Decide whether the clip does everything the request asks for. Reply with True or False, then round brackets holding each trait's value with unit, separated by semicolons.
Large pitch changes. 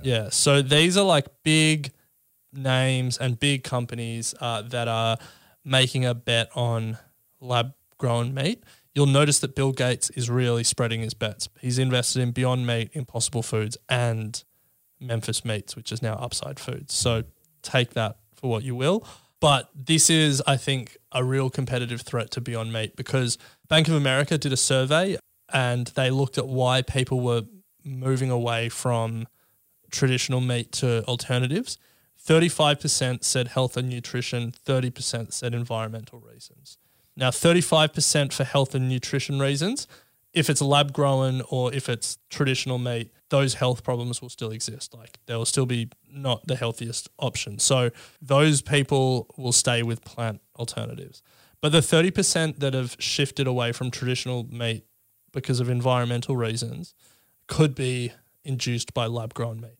False (2.8 semitones)